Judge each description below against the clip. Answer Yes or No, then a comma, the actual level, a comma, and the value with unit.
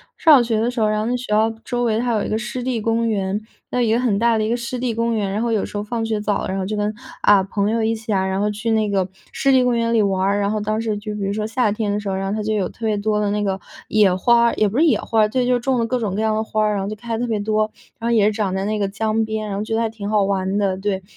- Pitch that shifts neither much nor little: No, narrow, 2.1 semitones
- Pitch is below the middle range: No, high, 215 Hz